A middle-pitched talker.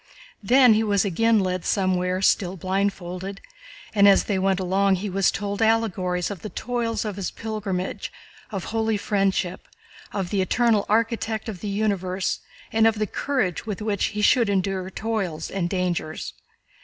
No: high, 200 Hz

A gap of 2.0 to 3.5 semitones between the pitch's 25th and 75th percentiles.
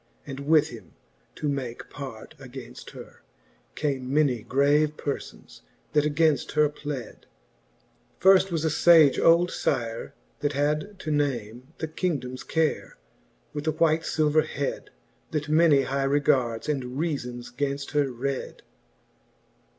Yes: average, 2.7 semitones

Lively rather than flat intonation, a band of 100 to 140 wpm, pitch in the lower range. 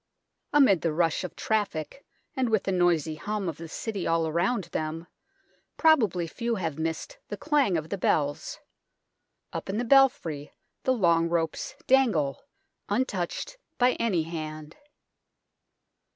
No: wide, 6.3 semitones; slow, 135 wpm; medium, 175 Hz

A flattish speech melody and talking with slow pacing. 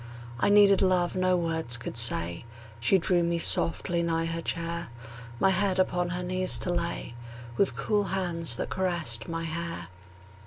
No: narrow, 2.0 semitones; average, 160 wpm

